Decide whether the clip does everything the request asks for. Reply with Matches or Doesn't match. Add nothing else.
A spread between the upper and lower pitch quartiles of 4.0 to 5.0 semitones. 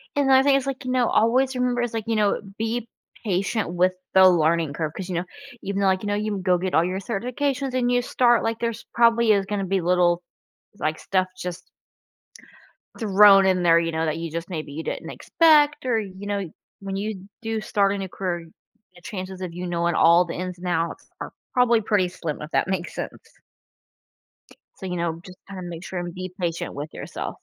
Matches